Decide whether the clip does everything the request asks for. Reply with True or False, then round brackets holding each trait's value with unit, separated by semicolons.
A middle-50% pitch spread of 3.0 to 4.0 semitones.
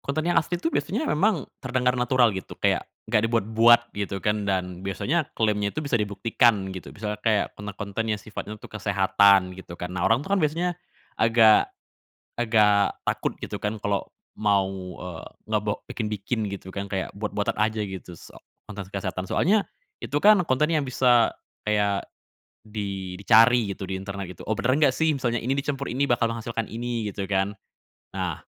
True (3.7 semitones)